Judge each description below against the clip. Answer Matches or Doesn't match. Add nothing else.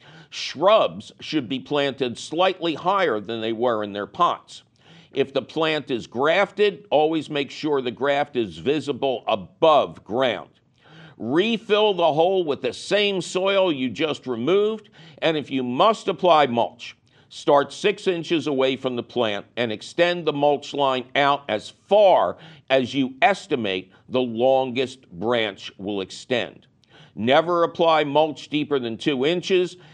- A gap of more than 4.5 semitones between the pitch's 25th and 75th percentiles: Matches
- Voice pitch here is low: Doesn't match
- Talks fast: Doesn't match